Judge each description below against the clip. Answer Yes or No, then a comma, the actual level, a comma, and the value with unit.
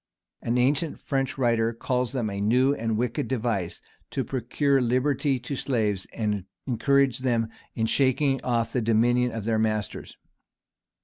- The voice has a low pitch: Yes, low, 120 Hz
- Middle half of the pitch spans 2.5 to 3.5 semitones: Yes, average, 2.9 semitones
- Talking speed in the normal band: Yes, average, 150 wpm